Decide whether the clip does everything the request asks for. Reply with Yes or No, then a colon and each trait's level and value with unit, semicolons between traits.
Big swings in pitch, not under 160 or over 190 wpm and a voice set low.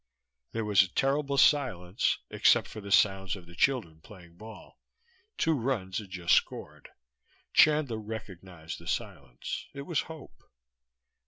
No: wide, 6.9 semitones; average, 140 wpm; low, 105 Hz